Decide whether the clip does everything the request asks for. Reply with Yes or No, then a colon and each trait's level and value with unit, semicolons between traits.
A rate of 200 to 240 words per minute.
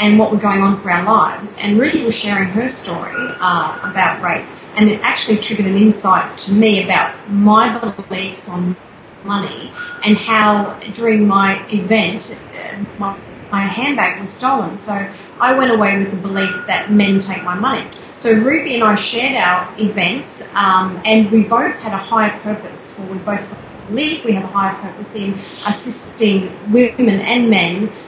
No: average, 175 wpm